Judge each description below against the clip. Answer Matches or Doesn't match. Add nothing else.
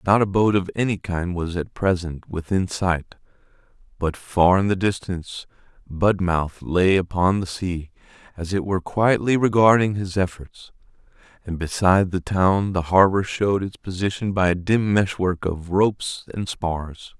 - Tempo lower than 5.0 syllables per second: Matches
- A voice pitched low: Matches